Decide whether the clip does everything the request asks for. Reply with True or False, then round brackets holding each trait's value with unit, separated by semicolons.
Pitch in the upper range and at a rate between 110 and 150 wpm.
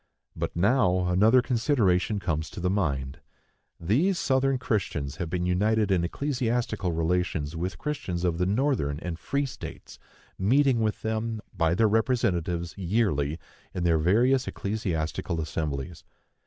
False (95 Hz; 135 wpm)